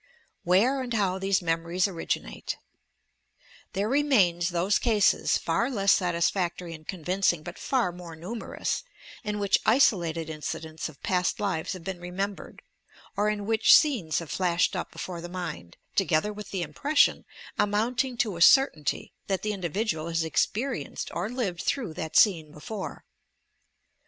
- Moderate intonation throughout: Yes, average, 4.0 semitones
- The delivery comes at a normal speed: Yes, average, 150 wpm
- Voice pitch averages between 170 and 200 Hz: Yes, medium, 185 Hz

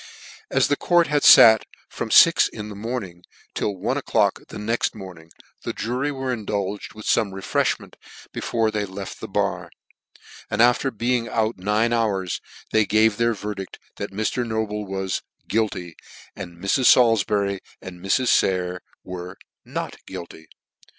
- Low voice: Yes, low, 105 Hz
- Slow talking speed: No, average, 155 wpm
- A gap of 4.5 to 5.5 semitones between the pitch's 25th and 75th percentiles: No, average, 3.2 semitones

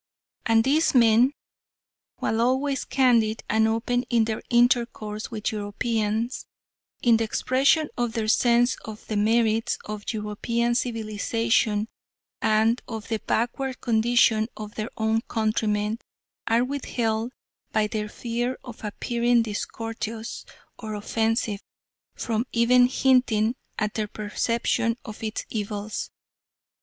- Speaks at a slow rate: Yes, slow, 120 wpm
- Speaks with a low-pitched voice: No, high, 225 Hz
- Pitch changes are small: Yes, narrow, 1.8 semitones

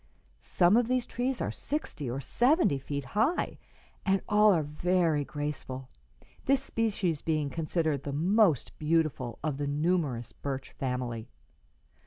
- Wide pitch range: Yes, wide, 6.8 semitones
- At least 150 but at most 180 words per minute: No, slow, 135 wpm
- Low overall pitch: No, medium, 155 Hz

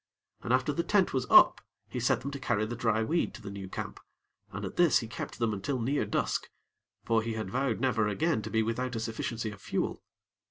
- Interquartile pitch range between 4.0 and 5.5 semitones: No, average, 3.2 semitones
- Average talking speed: No, fast, 230 wpm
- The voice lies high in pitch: No, low, 115 Hz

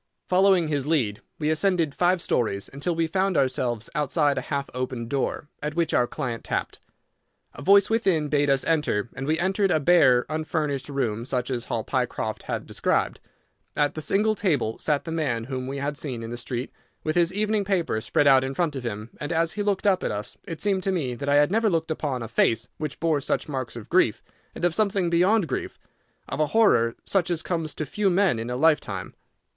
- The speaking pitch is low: No, medium, 150 Hz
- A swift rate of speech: Yes, fast, 215 wpm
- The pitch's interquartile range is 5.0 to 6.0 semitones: Yes, wide, 5.4 semitones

